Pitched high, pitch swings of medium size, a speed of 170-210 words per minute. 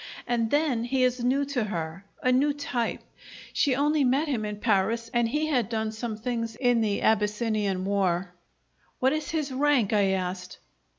Yes: high, 230 Hz; average, 4.2 semitones; average, 180 wpm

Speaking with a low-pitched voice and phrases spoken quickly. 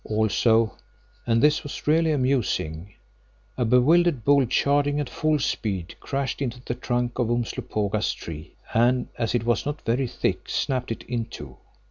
No: low, 120 Hz; average, 150 wpm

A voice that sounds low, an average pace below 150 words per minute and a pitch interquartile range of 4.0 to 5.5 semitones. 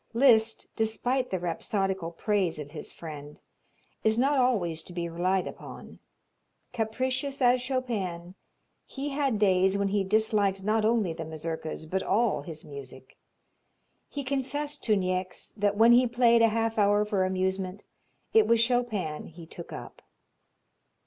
No: high, 205 Hz; average, 140 wpm; average, 4.9 semitones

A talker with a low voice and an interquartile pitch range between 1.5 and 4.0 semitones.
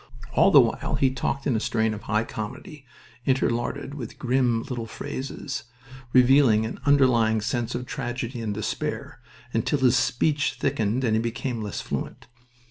Yes: low, 120 Hz; average, 3.0 semitones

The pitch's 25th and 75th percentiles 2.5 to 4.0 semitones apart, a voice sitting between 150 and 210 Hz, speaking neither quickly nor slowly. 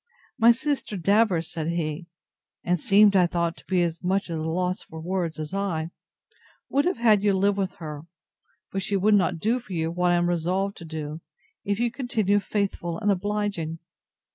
Yes: average, 3.6 semitones; medium, 185 Hz; average, 190 wpm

